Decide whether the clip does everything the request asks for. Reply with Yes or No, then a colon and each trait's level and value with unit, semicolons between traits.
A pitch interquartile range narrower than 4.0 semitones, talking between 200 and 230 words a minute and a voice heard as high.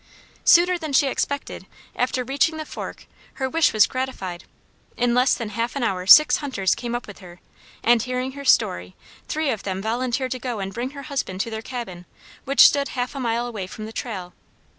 No: average, 4.4 semitones; fast, 205 wpm; high, 245 Hz